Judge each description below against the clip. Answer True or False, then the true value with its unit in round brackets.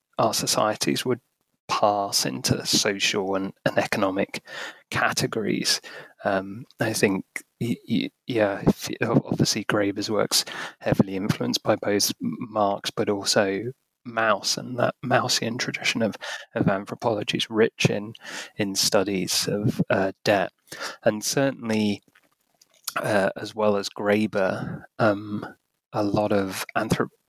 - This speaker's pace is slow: True (115 wpm)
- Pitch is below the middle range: True (105 Hz)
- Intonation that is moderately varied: False (1.1 semitones)